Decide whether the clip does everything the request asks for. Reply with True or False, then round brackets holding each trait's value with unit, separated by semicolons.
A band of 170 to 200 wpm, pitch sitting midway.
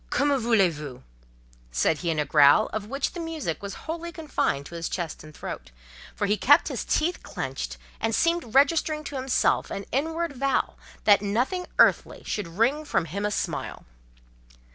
False (180 wpm; 225 Hz)